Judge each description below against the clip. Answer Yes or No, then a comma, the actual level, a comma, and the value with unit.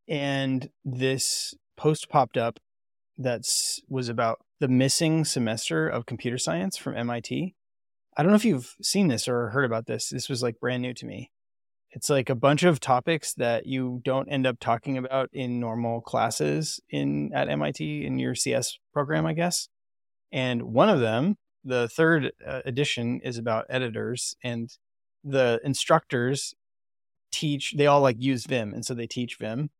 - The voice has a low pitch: Yes, low, 130 Hz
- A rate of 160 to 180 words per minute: Yes, average, 165 wpm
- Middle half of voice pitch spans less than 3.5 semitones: No, average, 3.8 semitones